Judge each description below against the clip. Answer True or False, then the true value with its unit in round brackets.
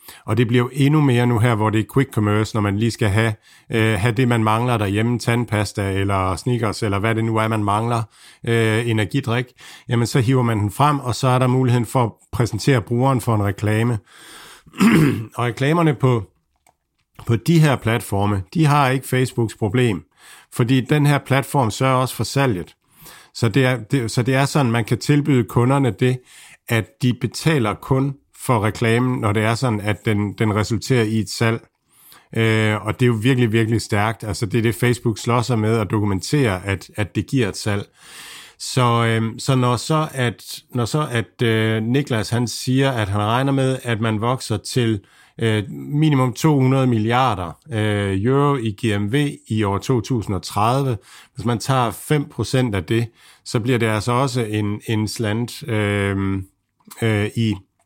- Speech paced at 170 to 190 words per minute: True (185 wpm)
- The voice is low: True (115 Hz)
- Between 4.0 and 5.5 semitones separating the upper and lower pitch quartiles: False (3.0 semitones)